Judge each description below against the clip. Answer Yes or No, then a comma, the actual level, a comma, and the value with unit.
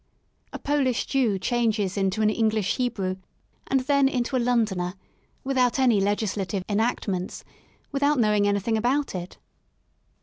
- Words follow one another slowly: Yes, slow, 130 wpm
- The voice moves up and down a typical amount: Yes, average, 4.2 semitones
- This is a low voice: No, high, 220 Hz